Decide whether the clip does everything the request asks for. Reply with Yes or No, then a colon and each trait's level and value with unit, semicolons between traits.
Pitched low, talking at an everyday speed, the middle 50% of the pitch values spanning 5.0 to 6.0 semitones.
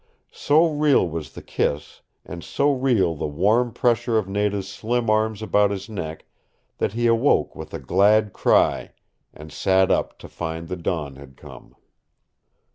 Yes: low, 100 Hz; average, 160 wpm; wide, 5.4 semitones